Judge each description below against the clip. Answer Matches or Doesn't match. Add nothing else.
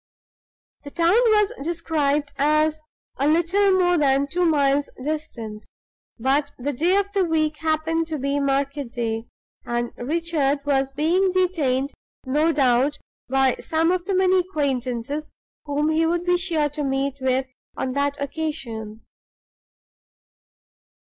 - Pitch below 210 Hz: Doesn't match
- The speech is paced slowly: Matches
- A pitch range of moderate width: Matches